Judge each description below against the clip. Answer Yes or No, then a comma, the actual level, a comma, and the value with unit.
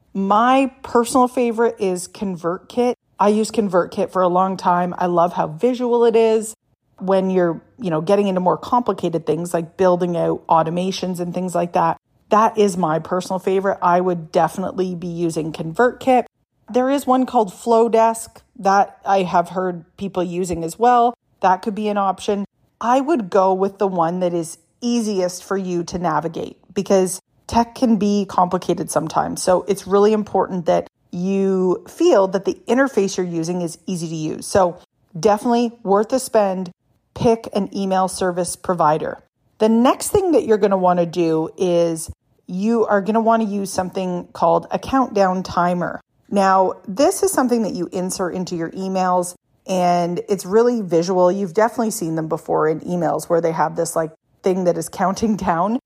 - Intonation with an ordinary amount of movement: Yes, average, 3.9 semitones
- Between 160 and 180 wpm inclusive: Yes, average, 175 wpm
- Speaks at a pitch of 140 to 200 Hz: Yes, high, 190 Hz